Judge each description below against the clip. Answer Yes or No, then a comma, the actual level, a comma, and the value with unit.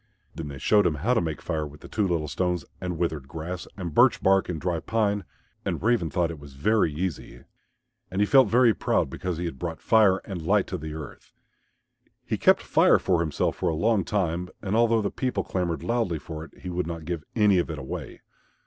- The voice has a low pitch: Yes, very low, 90 Hz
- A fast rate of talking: Yes, fast, 220 wpm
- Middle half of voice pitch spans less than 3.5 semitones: No, average, 4.3 semitones